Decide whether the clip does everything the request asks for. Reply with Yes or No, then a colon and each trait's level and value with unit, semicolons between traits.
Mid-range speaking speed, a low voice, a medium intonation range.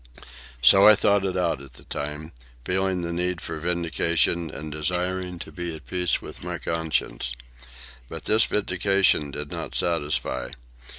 Yes: average, 155 wpm; very low, 85 Hz; average, 3.1 semitones